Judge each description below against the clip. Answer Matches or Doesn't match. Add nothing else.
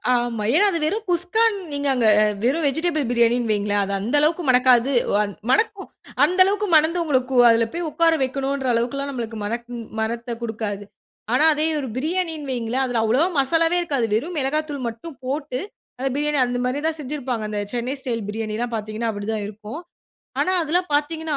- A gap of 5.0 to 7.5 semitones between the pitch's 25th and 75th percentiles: Matches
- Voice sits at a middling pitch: Doesn't match